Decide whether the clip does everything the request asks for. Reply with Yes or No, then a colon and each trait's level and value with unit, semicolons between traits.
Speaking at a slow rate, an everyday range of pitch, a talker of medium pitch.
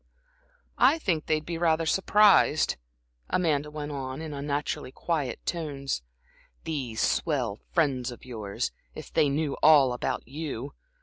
Yes: slow, 130 wpm; average, 3.4 semitones; medium, 145 Hz